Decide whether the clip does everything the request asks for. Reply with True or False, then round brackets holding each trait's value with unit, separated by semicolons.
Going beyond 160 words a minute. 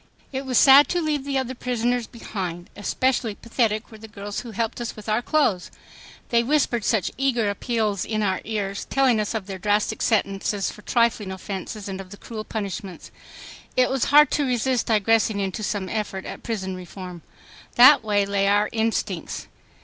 True (180 wpm)